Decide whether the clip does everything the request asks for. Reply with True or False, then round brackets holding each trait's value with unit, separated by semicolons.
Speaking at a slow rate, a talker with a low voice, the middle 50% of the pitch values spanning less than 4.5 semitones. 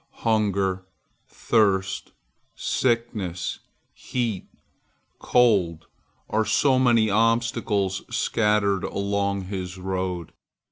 True (75 wpm; 100 Hz; 3.3 semitones)